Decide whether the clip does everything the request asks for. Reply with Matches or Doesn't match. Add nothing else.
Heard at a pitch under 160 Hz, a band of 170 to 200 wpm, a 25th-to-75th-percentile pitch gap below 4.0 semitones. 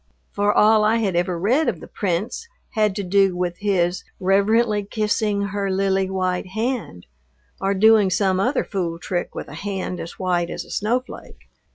Doesn't match